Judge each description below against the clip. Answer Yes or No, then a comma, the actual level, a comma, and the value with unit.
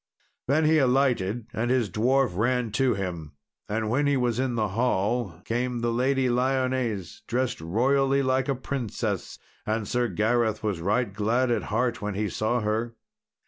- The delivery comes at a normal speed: Yes, average, 165 wpm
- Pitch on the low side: Yes, low, 120 Hz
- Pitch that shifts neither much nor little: Yes, average, 3.3 semitones